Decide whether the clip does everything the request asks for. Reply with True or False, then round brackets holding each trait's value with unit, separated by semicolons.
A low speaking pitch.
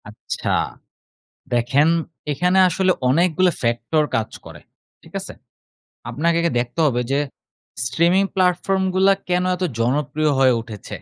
False (155 Hz)